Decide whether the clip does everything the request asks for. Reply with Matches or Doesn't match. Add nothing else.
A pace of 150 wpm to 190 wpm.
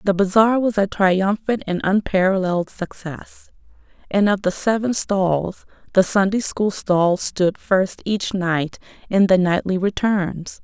Doesn't match